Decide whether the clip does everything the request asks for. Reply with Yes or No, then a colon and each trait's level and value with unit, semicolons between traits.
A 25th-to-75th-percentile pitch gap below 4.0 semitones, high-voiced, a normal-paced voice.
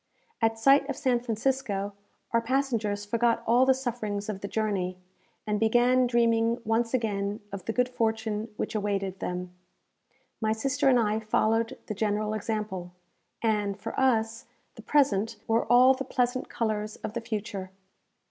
Yes: average, 2.7 semitones; high, 225 Hz; average, 155 wpm